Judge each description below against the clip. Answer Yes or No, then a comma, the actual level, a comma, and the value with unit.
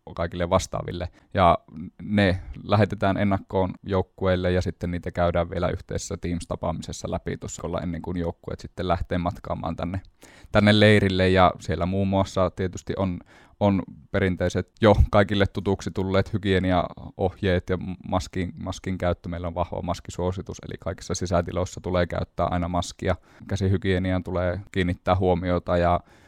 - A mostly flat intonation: Yes, narrow, 1.8 semitones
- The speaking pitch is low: Yes, very low, 90 Hz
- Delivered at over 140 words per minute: No, average, 130 wpm